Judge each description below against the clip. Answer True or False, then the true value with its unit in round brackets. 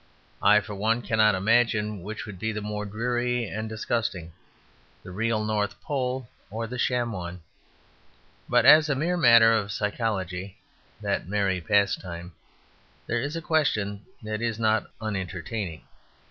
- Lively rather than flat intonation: False (2.8 semitones)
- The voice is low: True (110 Hz)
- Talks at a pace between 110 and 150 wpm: True (145 wpm)